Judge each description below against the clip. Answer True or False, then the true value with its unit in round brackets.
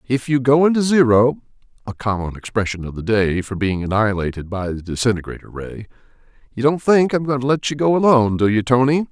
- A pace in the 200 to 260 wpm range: True (205 wpm)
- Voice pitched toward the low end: True (120 Hz)